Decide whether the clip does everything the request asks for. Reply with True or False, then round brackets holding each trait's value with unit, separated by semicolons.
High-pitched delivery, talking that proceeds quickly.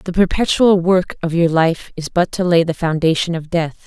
False (170 Hz; 220 wpm)